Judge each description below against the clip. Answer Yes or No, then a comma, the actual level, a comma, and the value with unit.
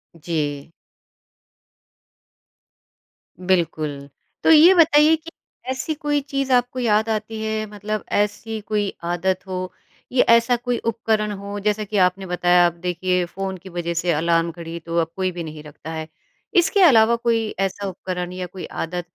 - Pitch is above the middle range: Yes, high, 195 Hz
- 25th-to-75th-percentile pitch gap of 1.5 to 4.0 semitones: No, average, 4.7 semitones